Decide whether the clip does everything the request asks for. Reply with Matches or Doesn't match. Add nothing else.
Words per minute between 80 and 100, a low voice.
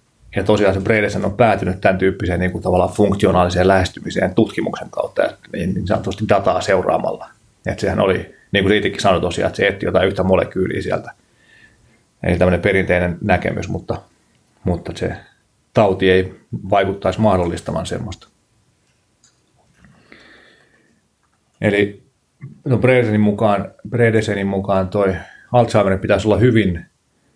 Doesn't match